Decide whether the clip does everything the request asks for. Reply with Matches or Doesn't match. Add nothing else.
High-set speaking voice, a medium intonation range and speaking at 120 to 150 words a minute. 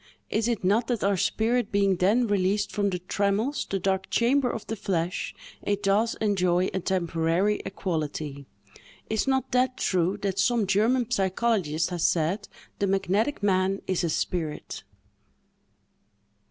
Matches